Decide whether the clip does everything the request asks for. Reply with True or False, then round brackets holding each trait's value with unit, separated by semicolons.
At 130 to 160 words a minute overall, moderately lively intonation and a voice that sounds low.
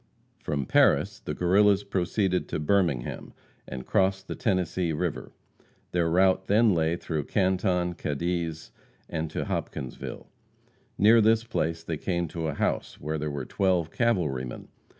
True (140 wpm; 3.5 semitones; 90 Hz)